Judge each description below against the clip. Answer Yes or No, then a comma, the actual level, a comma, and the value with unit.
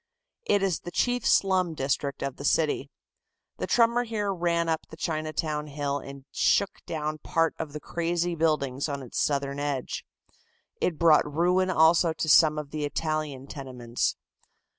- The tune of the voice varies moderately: Yes, average, 3.2 semitones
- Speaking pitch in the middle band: Yes, medium, 155 Hz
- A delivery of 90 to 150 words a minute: No, average, 160 wpm